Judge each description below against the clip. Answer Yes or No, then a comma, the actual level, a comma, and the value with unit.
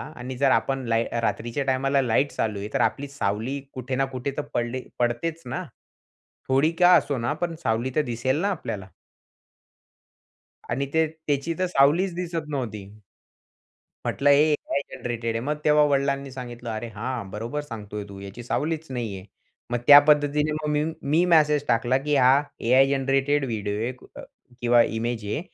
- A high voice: No, low, 135 Hz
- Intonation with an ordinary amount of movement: Yes, average, 3.7 semitones